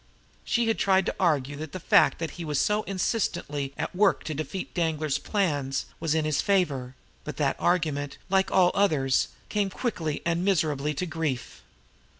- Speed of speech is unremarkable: Yes, average, 170 wpm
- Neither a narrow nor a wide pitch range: Yes, average, 4.6 semitones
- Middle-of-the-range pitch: Yes, medium, 160 Hz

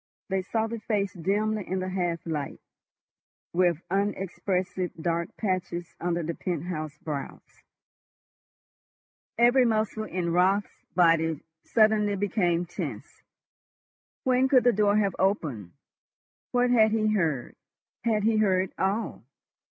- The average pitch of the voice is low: No, high, 190 Hz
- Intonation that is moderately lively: Yes, average, 4.0 semitones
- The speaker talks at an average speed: No, slow, 120 wpm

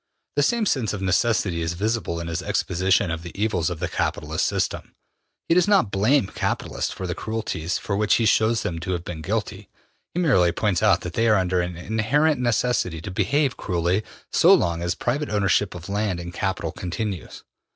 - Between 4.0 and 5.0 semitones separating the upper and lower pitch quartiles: Yes, average, 4.4 semitones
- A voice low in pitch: Yes, low, 100 Hz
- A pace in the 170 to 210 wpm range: Yes, average, 195 wpm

